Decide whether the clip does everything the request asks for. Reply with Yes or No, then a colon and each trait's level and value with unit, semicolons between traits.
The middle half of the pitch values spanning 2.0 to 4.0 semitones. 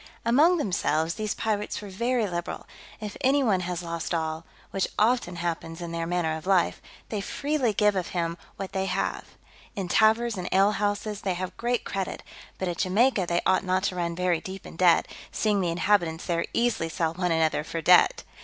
Yes: average, 3.6 semitones